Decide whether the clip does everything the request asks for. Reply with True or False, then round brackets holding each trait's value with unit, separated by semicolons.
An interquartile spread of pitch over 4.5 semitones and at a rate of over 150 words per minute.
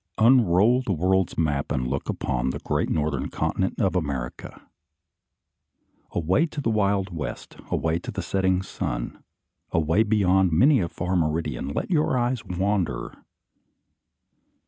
False (5.3 semitones; 135 wpm)